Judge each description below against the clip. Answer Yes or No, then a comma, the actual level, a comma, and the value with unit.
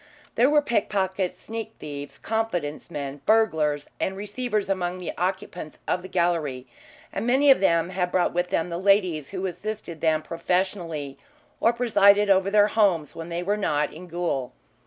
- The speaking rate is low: No, average, 165 wpm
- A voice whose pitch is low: No, medium, 185 Hz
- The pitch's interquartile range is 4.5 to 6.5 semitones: No, average, 4.0 semitones